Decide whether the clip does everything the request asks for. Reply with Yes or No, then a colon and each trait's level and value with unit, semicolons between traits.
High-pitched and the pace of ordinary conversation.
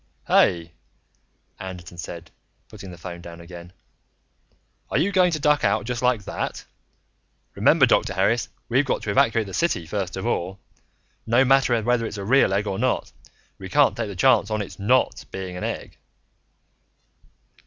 No: low, 100 Hz; average, 165 wpm